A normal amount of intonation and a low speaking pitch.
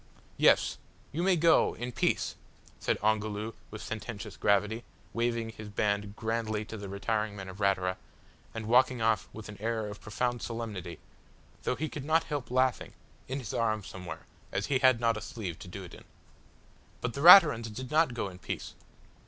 Yes: average, 3.3 semitones; low, 110 Hz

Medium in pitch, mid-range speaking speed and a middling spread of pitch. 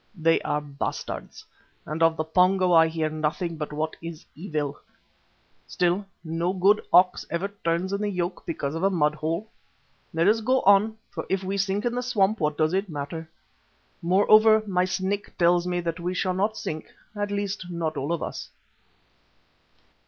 Yes: medium, 180 Hz; average, 175 wpm; average, 3.5 semitones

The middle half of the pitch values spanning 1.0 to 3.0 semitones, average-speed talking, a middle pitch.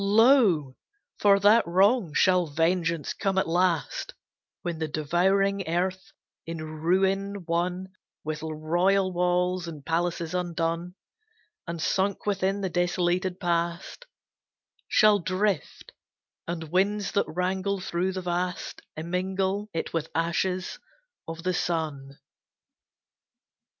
No: narrow, 2.4 semitones; slow, 110 wpm; medium, 180 Hz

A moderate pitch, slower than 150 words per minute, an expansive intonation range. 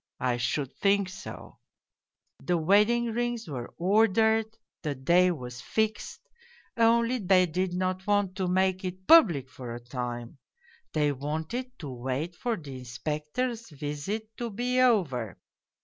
Yes: medium, 180 Hz; slow, 135 wpm; wide, 7.6 semitones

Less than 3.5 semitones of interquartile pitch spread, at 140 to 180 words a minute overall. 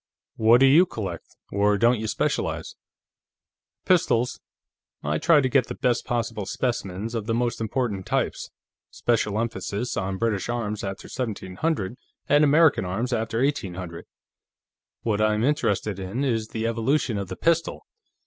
No: average, 3.8 semitones; average, 145 wpm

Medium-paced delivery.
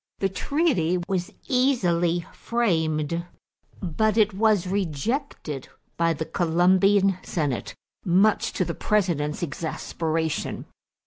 No: slow, 100 wpm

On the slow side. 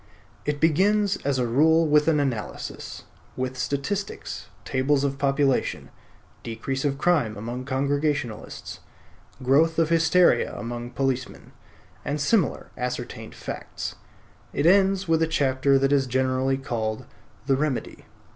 Yes: slow, 125 wpm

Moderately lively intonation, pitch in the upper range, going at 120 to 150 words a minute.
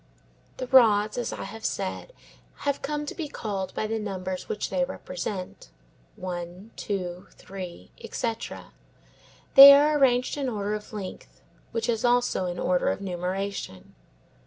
Yes: average, 4.9 semitones; high, 210 Hz; average, 145 wpm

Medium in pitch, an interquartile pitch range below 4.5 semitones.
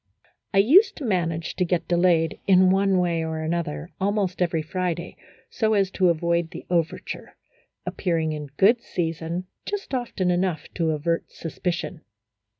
Yes: medium, 175 Hz; average, 2.7 semitones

